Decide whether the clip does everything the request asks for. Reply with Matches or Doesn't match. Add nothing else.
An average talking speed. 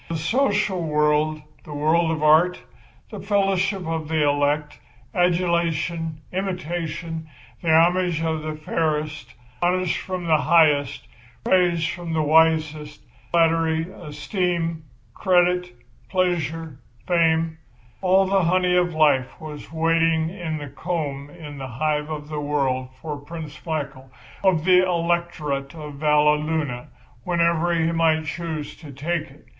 Doesn't match